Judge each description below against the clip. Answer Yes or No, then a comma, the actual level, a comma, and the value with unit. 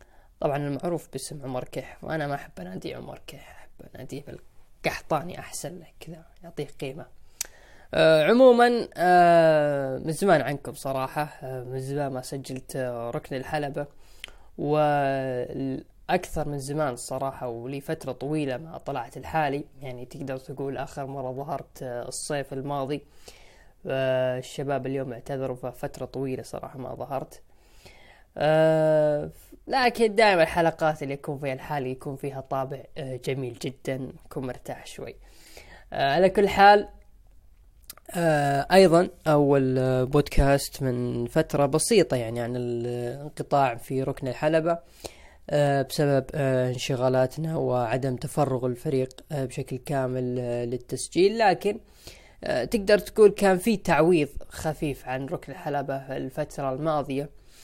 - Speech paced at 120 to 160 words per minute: No, average, 110 wpm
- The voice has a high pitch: No, medium, 140 Hz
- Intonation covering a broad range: No, average, 3.0 semitones